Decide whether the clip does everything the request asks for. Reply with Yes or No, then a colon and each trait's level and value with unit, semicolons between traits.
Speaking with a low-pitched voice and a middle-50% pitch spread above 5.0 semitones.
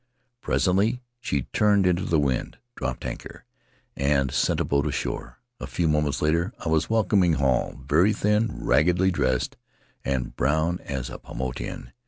Yes: very low, 80 Hz; wide, 5.6 semitones